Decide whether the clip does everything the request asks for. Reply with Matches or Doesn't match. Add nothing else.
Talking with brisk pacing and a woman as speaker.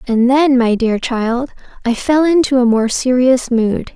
Doesn't match